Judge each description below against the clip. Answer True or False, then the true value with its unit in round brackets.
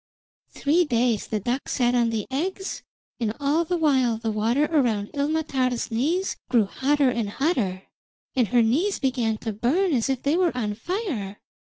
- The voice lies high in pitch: True (255 Hz)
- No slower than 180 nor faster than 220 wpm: False (170 wpm)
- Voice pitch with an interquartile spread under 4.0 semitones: False (5.1 semitones)